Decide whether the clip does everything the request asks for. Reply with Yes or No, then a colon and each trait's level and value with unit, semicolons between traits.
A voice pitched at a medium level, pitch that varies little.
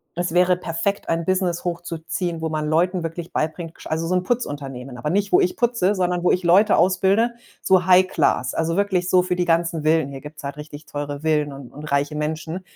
No: medium, 170 Hz; average, 3.1 semitones